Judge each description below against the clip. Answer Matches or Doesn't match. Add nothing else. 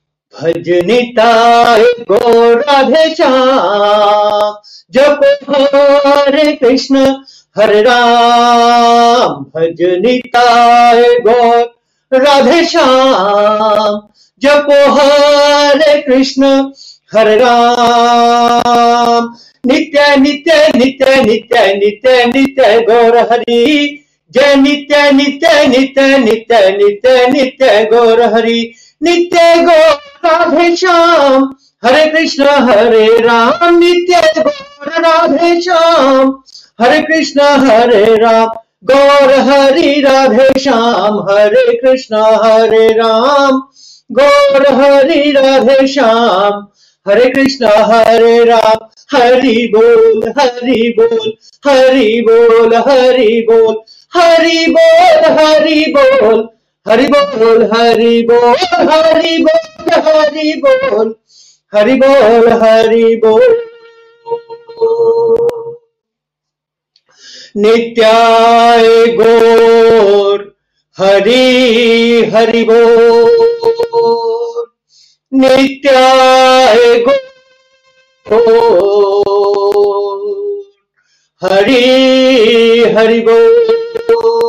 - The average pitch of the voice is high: Matches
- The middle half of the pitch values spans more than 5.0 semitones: Doesn't match